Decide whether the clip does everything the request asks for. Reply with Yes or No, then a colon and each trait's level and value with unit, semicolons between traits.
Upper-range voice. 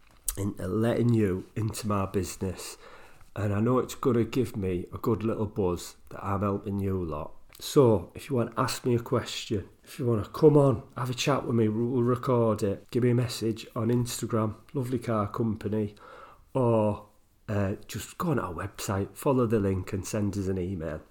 No: low, 110 Hz